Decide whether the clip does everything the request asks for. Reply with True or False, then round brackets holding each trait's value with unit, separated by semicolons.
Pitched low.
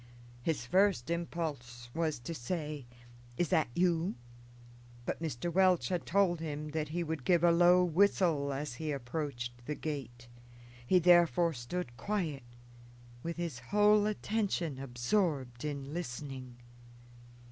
False (160 Hz)